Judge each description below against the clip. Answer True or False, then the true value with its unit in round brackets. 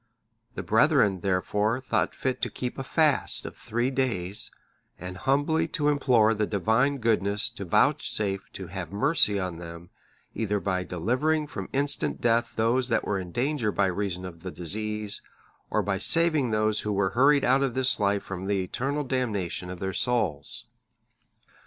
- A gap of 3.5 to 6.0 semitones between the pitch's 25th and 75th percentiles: True (5.4 semitones)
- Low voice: True (110 Hz)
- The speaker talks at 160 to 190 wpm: True (165 wpm)